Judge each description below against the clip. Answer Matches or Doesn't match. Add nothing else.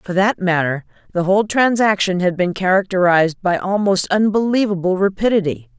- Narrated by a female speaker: Matches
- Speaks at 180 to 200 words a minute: Doesn't match